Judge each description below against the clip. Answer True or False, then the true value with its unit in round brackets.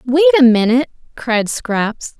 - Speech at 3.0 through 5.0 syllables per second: True (4.2 syllables/s)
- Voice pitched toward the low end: False (230 Hz)